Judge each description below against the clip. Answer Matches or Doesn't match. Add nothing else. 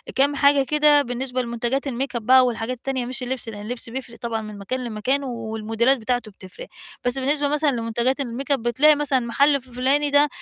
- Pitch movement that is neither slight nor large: Matches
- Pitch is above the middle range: Matches